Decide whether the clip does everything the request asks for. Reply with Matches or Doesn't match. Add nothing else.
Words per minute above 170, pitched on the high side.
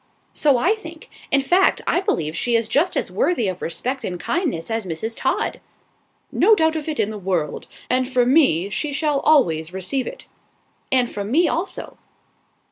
Matches